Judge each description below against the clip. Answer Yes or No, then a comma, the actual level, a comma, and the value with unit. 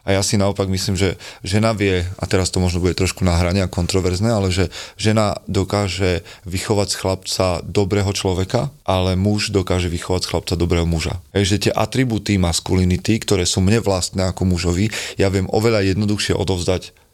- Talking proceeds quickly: Yes, fast, 170 wpm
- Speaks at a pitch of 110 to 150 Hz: No, very low, 95 Hz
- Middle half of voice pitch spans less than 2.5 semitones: Yes, narrow, 2.1 semitones